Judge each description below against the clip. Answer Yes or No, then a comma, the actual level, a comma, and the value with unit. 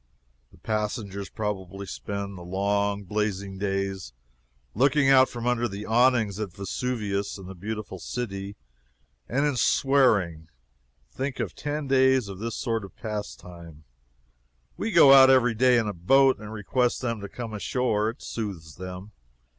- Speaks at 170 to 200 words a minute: No, average, 150 wpm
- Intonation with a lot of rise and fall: No, average, 4.1 semitones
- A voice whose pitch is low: Yes, low, 105 Hz